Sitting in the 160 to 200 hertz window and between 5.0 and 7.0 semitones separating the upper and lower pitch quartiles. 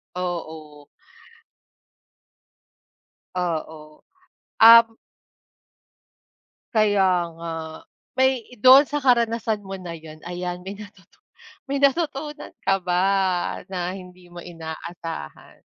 Yes: medium, 185 Hz; average, 5.3 semitones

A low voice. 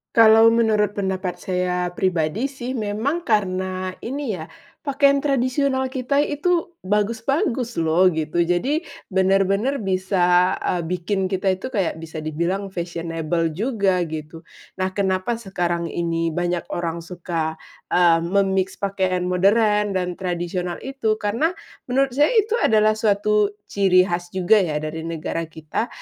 No: high, 190 Hz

